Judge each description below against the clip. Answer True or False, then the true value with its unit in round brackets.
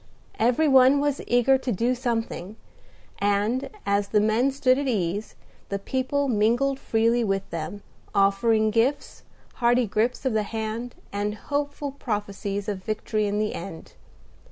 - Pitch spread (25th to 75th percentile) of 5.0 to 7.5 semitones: False (3.9 semitones)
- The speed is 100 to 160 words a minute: True (145 wpm)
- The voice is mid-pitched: False (225 Hz)